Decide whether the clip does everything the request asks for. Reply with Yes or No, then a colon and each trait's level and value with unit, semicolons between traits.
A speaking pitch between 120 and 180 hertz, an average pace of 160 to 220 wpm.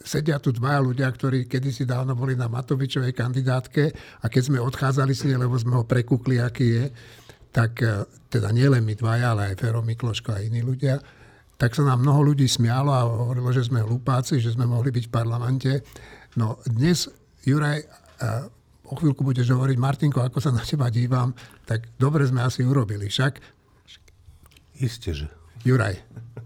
Yes: low, 125 Hz; fast, 165 wpm